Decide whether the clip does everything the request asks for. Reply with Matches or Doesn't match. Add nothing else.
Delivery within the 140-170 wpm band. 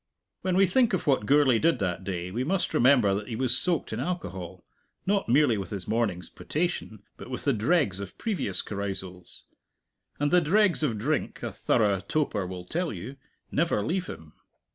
Doesn't match